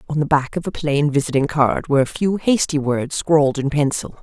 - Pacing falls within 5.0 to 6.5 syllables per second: Yes, 5.4 syllables/s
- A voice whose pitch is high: No, medium, 145 Hz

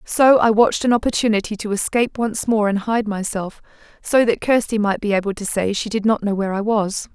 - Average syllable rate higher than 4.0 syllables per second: Yes, 5.7 syllables/s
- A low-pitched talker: No, high, 215 Hz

